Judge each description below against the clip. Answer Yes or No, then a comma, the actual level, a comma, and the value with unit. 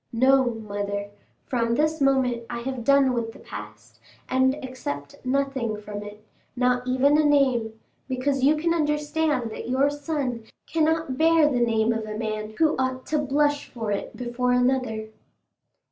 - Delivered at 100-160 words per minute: Yes, average, 155 wpm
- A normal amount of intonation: Yes, average, 4.0 semitones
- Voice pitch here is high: Yes, very high, 255 Hz